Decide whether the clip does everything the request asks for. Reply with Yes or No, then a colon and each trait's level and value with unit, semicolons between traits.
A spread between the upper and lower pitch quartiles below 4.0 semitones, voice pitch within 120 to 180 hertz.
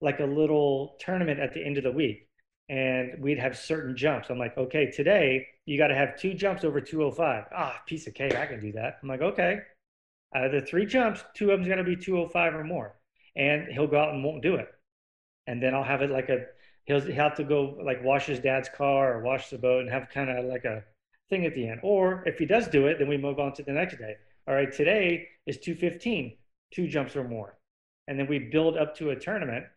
Yes: average, 3.4 semitones; medium, 140 Hz